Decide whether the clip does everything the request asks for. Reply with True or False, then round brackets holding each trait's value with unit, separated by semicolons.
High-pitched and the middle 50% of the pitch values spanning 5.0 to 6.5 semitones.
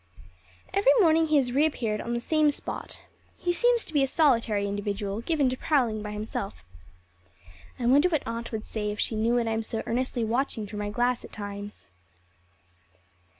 True (235 Hz; 5.3 semitones)